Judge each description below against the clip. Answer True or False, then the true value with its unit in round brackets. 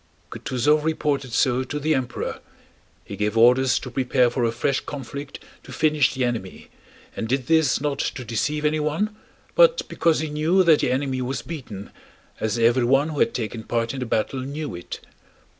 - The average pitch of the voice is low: True (130 Hz)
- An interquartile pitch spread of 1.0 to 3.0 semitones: False (3.9 semitones)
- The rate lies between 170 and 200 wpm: True (175 wpm)